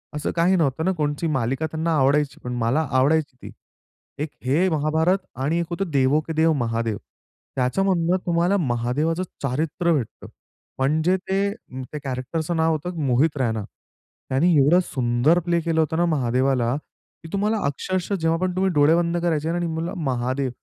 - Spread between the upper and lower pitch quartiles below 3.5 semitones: No, average, 4.4 semitones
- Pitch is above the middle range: No, medium, 155 Hz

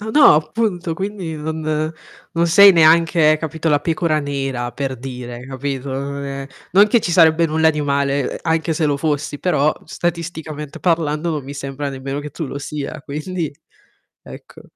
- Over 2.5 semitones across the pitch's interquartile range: Yes, average, 2.9 semitones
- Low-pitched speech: No, medium, 155 Hz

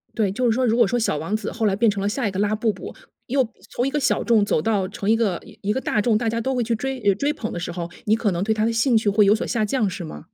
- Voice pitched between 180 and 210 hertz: No, high, 220 Hz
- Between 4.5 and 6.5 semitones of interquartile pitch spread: No, average, 2.8 semitones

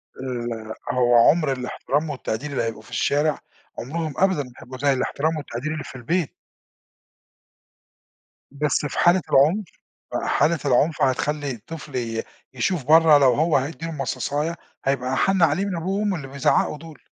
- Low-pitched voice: No, medium, 145 Hz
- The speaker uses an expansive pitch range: No, average, 4.0 semitones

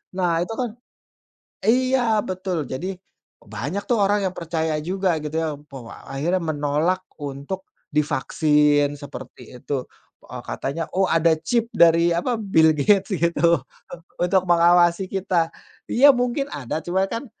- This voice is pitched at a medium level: Yes, medium, 170 Hz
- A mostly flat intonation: No, average, 4.2 semitones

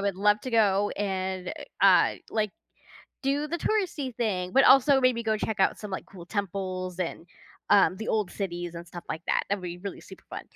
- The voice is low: No, high, 200 Hz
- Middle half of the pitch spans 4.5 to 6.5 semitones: No, average, 3.8 semitones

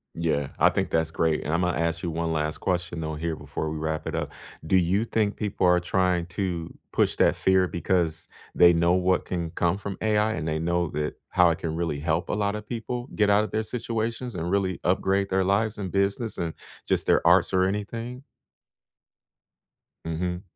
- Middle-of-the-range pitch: No, very low, 90 Hz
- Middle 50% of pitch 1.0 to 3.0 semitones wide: No, average, 3.5 semitones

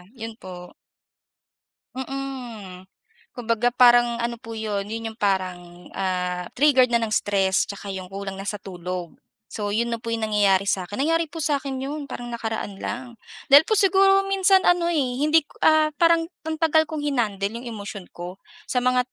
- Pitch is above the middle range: Yes, high, 230 Hz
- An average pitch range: No, wide, 6.3 semitones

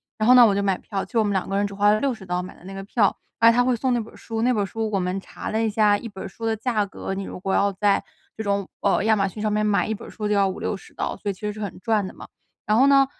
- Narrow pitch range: Yes, narrow, 2.2 semitones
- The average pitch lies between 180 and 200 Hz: No, high, 210 Hz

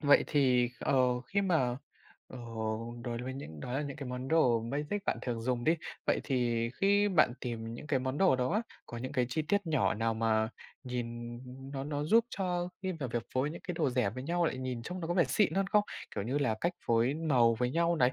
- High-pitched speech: No, low, 130 Hz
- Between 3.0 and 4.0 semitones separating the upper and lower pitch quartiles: No, average, 5.3 semitones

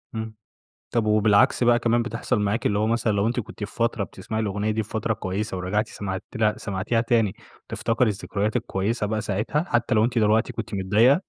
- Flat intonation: Yes, narrow, 2.1 semitones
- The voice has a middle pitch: No, low, 110 Hz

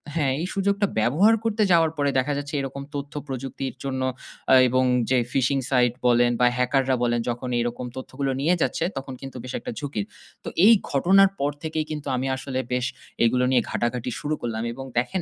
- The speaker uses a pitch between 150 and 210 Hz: No, low, 135 Hz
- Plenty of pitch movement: No, average, 3.0 semitones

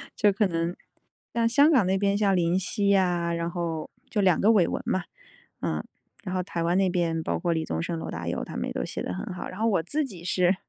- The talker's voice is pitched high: No, medium, 180 Hz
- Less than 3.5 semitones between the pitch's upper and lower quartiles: Yes, average, 3.0 semitones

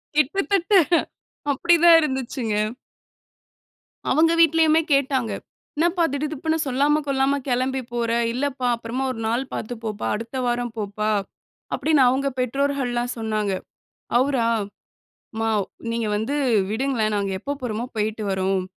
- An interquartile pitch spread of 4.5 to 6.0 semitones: No, average, 4.1 semitones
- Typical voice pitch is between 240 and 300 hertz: Yes, very high, 255 Hz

